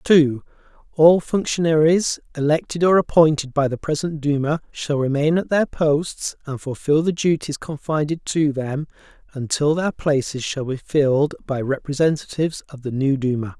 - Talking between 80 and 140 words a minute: No, average, 150 wpm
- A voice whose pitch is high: No, medium, 150 Hz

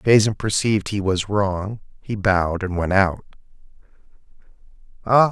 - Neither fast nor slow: No, slow, 115 wpm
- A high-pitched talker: No, low, 100 Hz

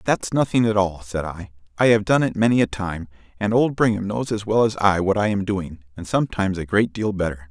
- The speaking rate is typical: No, fast, 250 wpm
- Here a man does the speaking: Yes, male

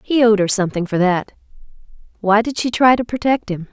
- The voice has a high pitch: Yes, high, 215 Hz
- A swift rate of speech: No, average, 195 wpm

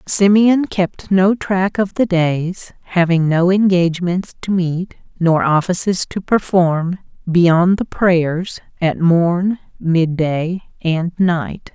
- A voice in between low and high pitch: Yes, medium, 180 Hz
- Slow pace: Yes, slow, 125 wpm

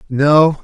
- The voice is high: No, medium, 145 Hz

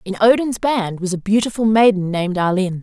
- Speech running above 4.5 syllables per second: Yes, 5.6 syllables/s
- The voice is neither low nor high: No, high, 205 Hz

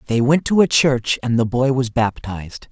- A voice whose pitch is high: No, low, 125 Hz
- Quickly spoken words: Yes, fast, 220 wpm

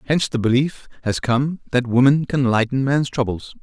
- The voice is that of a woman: No, male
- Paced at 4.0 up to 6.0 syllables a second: Yes, 5.1 syllables/s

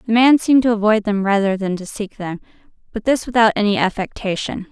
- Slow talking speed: No, fast, 205 wpm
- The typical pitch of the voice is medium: No, high, 215 Hz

